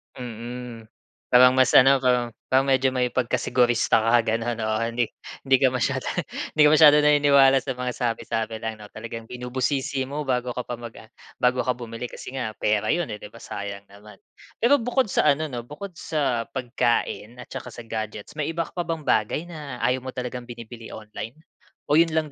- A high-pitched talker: No, low, 125 Hz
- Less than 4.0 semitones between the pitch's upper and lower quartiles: Yes, average, 3.0 semitones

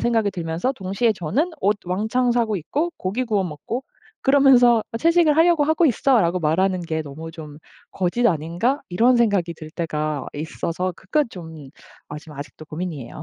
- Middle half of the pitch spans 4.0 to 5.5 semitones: No, wide, 7.1 semitones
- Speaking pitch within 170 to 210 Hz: Yes, high, 190 Hz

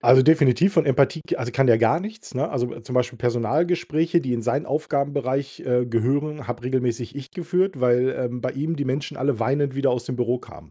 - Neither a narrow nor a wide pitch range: Yes, average, 3.3 semitones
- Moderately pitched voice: No, low, 130 Hz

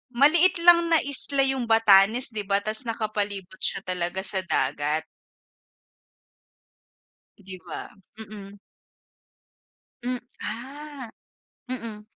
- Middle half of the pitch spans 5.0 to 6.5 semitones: Yes, average, 5.3 semitones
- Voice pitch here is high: Yes, high, 220 Hz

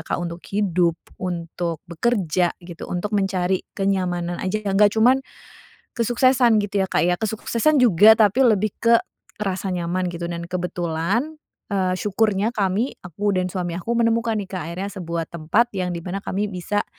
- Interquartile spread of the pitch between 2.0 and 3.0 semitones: No, average, 3.5 semitones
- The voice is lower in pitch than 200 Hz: Yes, high, 190 Hz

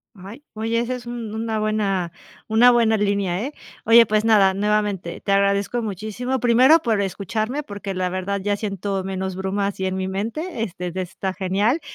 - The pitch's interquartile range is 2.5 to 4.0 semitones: Yes, average, 2.9 semitones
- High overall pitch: Yes, high, 205 Hz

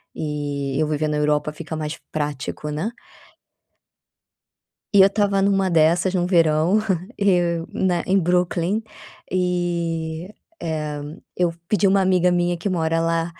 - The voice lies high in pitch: No, medium, 170 Hz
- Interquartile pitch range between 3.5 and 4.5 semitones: No, average, 2.9 semitones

